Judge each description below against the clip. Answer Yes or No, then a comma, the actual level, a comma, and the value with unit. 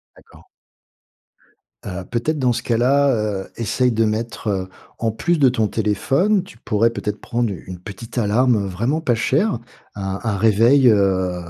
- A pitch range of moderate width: Yes, average, 3.7 semitones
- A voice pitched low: Yes, low, 115 Hz